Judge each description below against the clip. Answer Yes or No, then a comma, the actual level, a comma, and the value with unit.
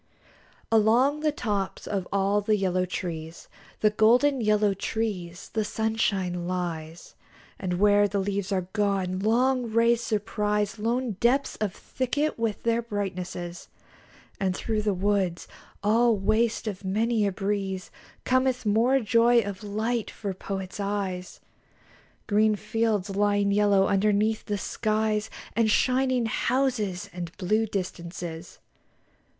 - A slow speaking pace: Yes, slow, 125 wpm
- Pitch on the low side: No, high, 210 Hz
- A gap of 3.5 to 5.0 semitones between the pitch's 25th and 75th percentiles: No, average, 2.9 semitones